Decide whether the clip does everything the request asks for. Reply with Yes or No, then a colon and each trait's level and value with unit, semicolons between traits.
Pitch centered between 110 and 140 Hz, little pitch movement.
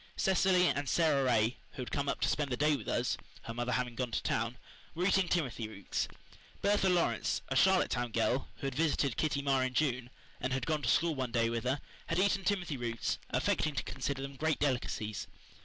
No: low, 135 Hz; average, 4.7 semitones